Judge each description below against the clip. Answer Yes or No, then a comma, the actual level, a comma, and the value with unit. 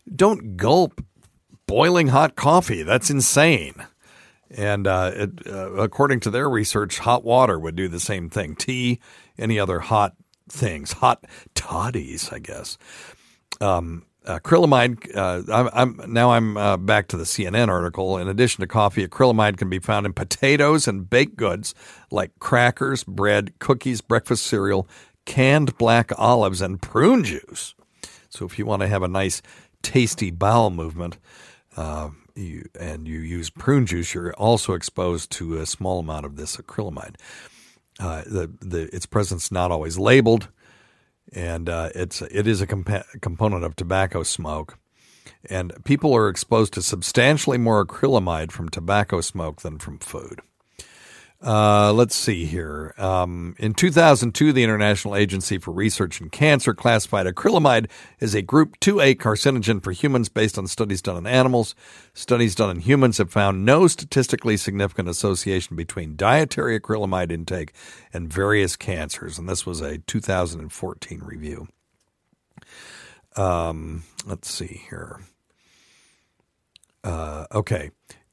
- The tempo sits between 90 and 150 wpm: Yes, average, 145 wpm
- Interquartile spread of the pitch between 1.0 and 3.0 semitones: No, average, 4.9 semitones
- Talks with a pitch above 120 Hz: No, low, 100 Hz